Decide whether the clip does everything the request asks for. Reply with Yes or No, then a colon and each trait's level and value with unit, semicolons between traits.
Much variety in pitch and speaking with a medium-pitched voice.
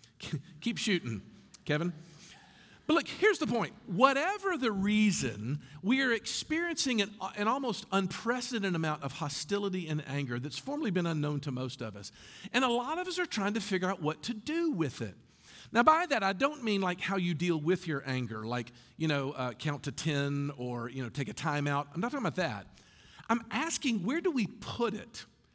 Yes: wide, 8.8 semitones; medium, 180 Hz